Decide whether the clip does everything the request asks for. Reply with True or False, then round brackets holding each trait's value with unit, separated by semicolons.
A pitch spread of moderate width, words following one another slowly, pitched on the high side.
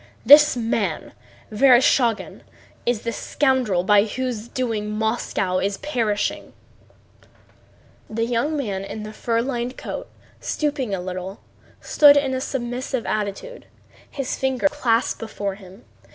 True (4.0 semitones; 125 wpm; 230 Hz)